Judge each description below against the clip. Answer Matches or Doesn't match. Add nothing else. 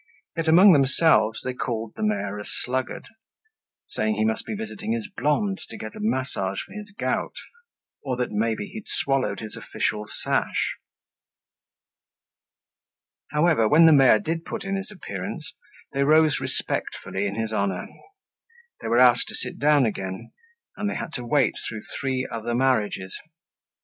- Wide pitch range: Matches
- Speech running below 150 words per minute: Doesn't match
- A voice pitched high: Doesn't match